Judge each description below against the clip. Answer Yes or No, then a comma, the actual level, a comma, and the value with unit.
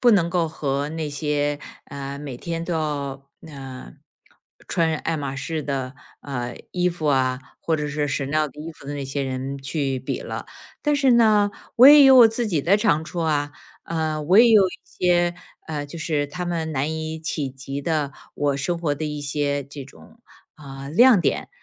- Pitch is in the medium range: Yes, medium, 150 Hz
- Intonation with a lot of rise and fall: No, average, 3.4 semitones